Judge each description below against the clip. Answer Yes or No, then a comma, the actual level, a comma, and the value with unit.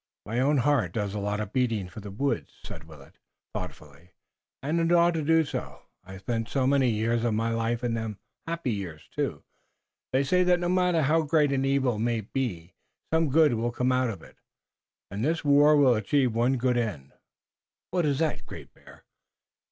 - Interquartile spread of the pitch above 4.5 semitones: Yes, average, 5.3 semitones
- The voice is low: Yes, low, 125 Hz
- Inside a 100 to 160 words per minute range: No, average, 195 wpm